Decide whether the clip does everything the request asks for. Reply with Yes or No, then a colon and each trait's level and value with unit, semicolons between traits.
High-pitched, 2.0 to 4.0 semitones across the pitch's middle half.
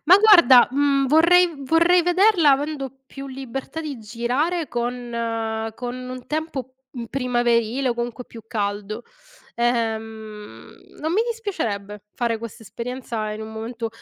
No: high, 245 Hz; average, 4.8 semitones